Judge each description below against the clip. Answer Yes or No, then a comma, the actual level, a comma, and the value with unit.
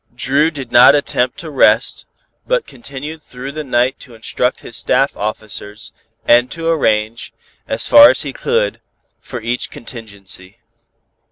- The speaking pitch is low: Yes, low, 125 Hz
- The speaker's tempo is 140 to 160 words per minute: Yes, average, 145 wpm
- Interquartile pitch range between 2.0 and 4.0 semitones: No, average, 4.7 semitones